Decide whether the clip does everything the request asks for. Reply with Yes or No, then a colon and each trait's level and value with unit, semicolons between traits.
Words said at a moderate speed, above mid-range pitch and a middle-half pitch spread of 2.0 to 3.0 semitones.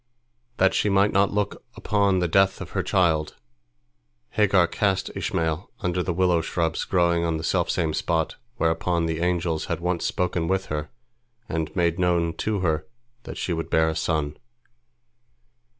No: average, 160 wpm; very low, 85 Hz; narrow, 2.4 semitones